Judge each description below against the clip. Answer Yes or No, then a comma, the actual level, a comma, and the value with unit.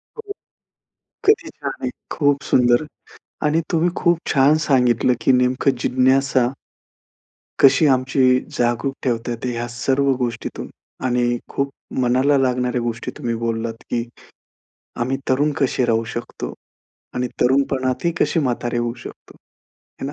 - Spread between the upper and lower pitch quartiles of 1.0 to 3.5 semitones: Yes, narrow, 2.4 semitones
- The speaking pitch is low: Yes, low, 130 Hz